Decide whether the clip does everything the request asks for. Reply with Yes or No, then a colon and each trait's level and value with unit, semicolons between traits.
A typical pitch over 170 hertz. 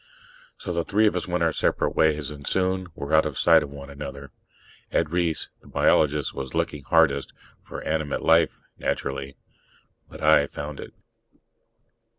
No: very low, 75 Hz